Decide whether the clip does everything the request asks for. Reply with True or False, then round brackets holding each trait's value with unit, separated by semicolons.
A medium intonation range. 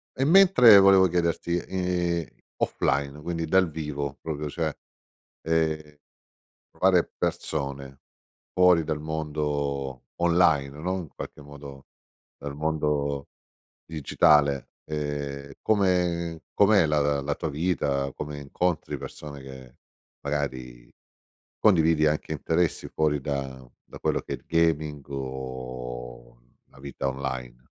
True (3.2 semitones)